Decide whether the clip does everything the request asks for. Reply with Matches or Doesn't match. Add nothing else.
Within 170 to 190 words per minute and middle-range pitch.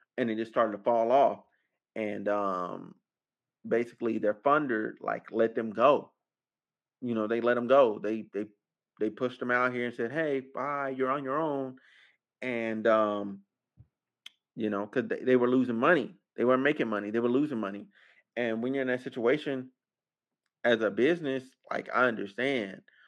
Doesn't match